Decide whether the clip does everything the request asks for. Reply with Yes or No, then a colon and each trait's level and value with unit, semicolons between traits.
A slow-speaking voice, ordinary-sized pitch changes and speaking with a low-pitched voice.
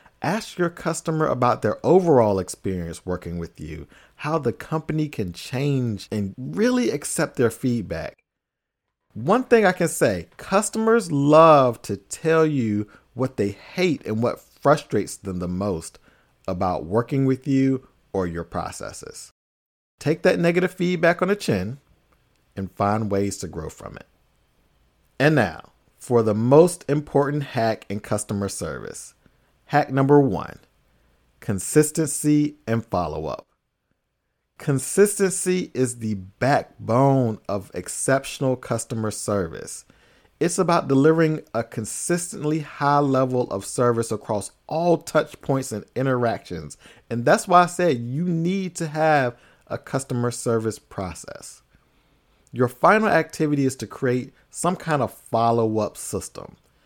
No: slow, 130 wpm; wide, 6.9 semitones; low, 130 Hz